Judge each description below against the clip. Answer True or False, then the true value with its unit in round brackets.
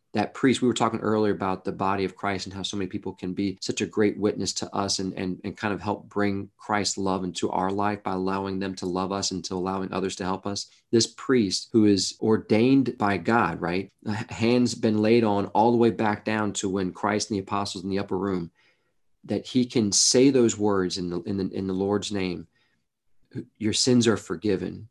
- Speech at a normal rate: False (225 wpm)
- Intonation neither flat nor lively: False (2.2 semitones)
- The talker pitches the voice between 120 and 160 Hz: False (100 Hz)